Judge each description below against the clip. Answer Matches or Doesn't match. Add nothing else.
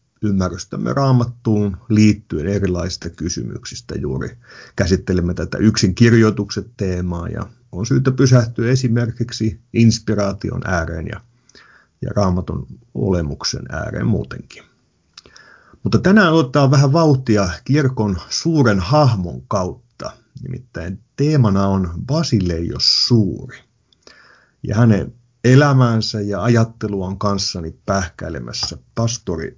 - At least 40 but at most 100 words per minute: Matches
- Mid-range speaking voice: Doesn't match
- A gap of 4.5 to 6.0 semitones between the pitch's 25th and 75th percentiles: Matches